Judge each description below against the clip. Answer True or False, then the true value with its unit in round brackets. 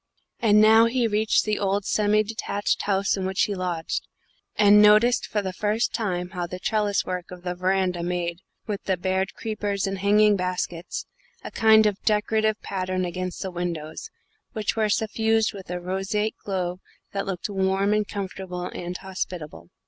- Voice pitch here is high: True (195 Hz)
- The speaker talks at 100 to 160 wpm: False (170 wpm)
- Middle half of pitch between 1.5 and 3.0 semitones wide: True (2.6 semitones)